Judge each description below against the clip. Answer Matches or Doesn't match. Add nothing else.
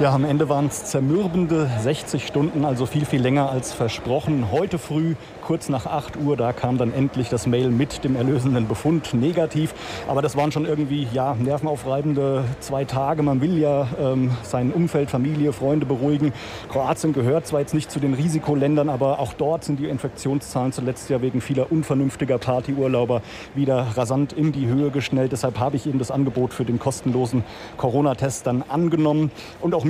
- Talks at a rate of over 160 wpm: Matches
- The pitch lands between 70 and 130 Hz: Doesn't match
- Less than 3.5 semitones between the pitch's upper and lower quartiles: Matches